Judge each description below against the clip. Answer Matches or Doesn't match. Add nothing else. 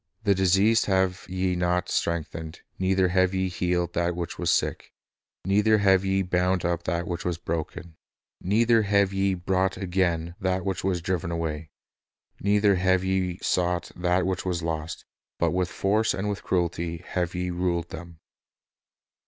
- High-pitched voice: Doesn't match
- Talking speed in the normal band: Matches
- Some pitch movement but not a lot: Doesn't match